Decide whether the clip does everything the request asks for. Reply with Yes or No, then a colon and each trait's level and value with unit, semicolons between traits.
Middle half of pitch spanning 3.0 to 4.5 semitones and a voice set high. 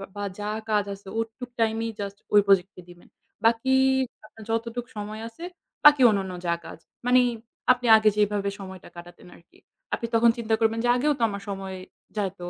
No: narrow, 2.6 semitones; high, 215 Hz